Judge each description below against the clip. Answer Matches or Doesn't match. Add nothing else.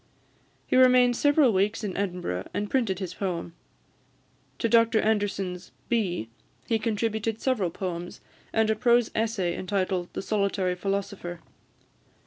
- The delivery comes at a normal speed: Doesn't match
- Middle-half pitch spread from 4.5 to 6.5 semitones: Doesn't match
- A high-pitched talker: Matches